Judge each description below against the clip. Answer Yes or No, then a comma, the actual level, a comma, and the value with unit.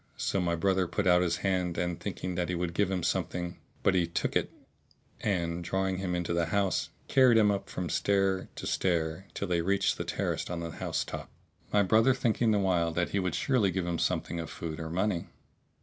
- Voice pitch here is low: Yes, very low, 90 Hz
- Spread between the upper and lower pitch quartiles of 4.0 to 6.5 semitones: No, narrow, 2.5 semitones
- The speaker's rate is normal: No, fast, 210 wpm